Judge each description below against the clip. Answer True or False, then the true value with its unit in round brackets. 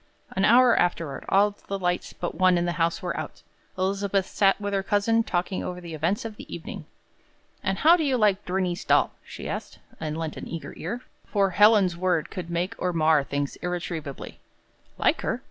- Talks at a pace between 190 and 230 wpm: True (195 wpm)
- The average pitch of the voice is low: False (185 Hz)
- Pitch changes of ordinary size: True (3.0 semitones)